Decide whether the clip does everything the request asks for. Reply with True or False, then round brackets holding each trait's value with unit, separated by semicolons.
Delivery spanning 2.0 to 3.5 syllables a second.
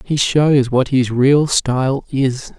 True (3.3 syllables/s)